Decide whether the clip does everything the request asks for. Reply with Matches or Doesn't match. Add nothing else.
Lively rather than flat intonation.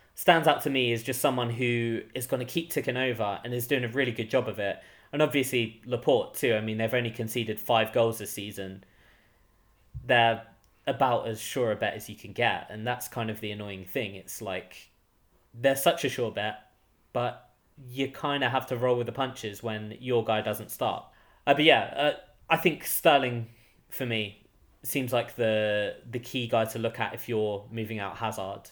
Doesn't match